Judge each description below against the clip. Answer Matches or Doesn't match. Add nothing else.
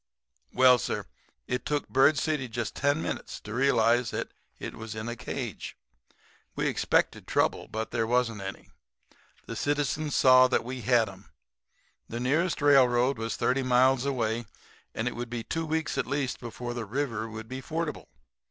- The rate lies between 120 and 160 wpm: Doesn't match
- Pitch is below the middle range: Matches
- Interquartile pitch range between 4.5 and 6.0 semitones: Doesn't match